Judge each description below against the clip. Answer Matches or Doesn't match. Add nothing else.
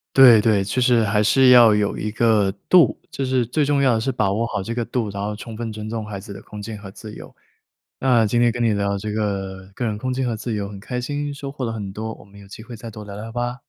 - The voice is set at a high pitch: Doesn't match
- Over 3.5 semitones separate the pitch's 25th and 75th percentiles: Doesn't match